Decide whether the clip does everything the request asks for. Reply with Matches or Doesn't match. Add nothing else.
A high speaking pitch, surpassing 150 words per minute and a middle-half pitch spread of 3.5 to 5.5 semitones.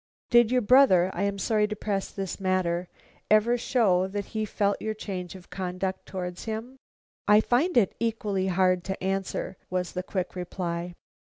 Doesn't match